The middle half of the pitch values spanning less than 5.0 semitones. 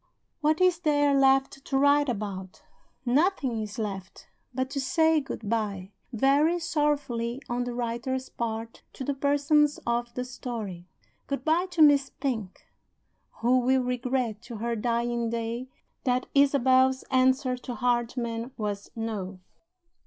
Yes: average, 3.3 semitones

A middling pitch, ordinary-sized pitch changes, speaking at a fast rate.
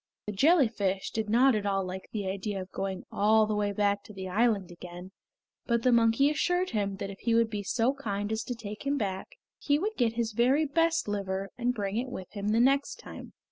No: high, 215 Hz; average, 3.8 semitones; fast, 225 wpm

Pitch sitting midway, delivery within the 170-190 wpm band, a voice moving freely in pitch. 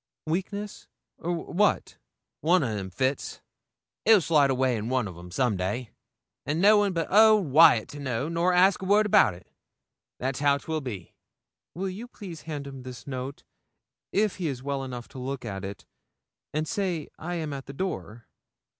Yes: medium, 145 Hz; average, 180 wpm; wide, 6.2 semitones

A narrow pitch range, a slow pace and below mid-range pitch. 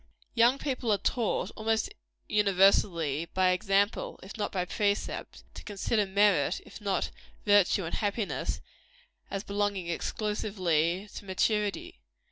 No: narrow, 2.3 semitones; slow, 120 wpm; high, 200 Hz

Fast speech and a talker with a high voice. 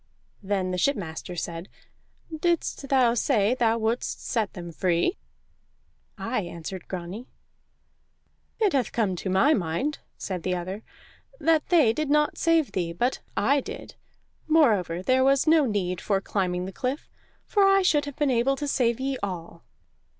No: average, 155 wpm; high, 230 Hz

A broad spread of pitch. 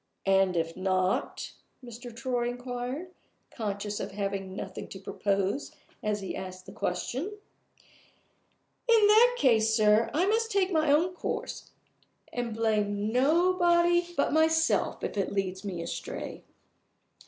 Yes: wide, 8.5 semitones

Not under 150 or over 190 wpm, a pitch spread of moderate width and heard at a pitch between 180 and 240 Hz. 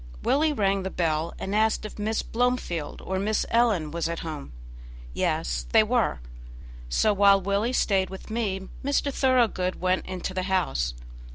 Yes: average, 160 wpm; average, 4.3 semitones; high, 190 Hz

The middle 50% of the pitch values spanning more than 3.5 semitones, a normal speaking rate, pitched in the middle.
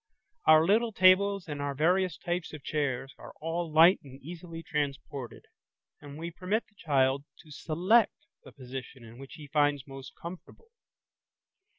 Yes: average, 4.3 semitones; average, 150 wpm; medium, 155 Hz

